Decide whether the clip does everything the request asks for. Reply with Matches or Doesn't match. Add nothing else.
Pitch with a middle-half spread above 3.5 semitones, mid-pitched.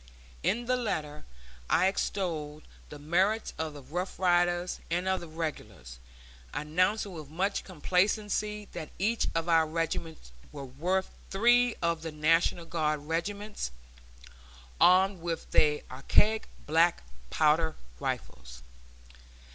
Matches